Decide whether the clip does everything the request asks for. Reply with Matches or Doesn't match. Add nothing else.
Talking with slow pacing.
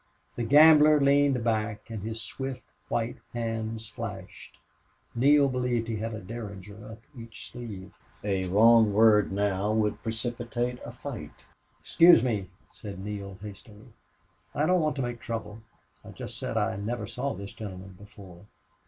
Doesn't match